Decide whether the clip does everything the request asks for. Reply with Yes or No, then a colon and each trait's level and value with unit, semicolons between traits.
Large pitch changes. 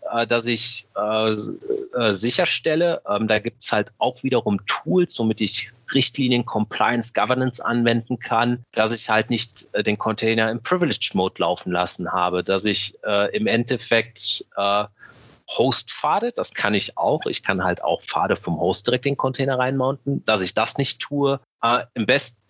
No: average, 3.3 semitones